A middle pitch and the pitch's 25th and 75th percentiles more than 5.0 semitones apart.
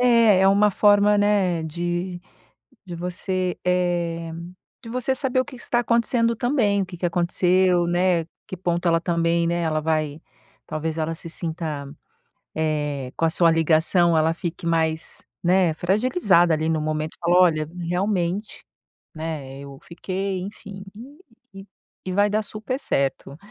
No: medium, 175 Hz; average, 3.5 semitones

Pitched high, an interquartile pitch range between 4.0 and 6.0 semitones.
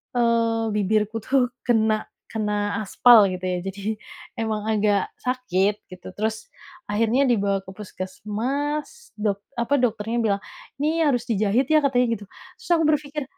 No: high, 220 Hz; average, 3.3 semitones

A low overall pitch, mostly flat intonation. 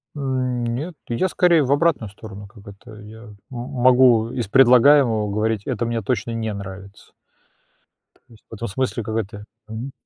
No: low, 115 Hz; average, 3.3 semitones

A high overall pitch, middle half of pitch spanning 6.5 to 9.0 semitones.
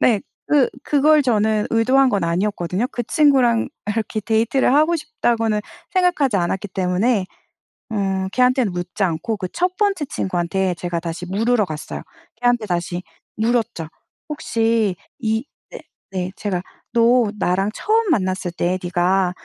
No: high, 215 Hz; average, 5.2 semitones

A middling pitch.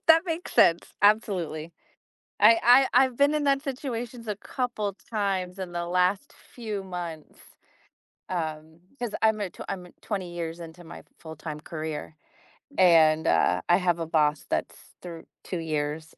Yes: medium, 180 Hz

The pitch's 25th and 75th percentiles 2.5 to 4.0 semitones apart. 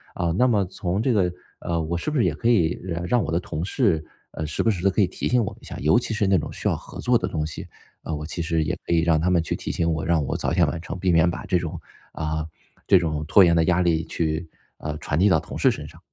Yes: average, 3.2 semitones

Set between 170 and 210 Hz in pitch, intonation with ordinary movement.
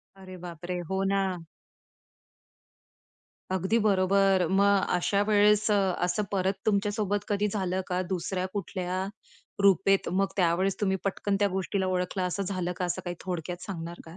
No: high, 190 Hz; narrow, 1.7 semitones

